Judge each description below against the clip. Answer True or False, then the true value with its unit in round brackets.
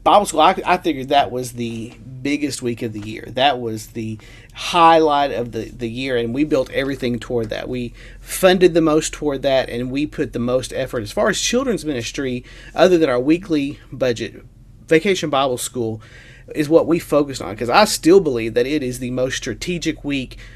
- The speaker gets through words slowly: False (200 wpm)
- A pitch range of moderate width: True (4.5 semitones)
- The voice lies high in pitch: False (130 Hz)